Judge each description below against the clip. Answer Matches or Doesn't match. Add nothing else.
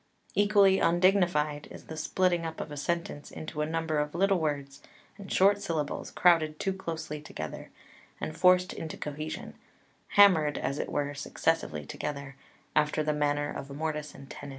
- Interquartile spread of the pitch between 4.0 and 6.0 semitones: Doesn't match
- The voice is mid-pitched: Matches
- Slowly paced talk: Doesn't match